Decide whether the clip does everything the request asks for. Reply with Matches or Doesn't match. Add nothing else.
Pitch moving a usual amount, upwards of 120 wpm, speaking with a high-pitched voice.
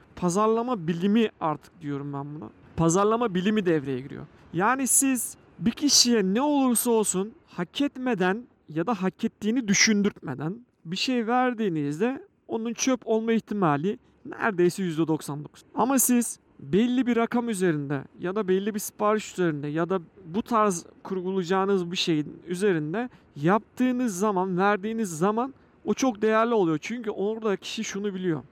Matches